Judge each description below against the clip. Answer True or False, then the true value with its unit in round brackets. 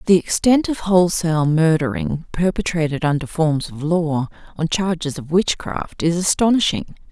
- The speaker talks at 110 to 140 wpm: True (135 wpm)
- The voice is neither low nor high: True (170 Hz)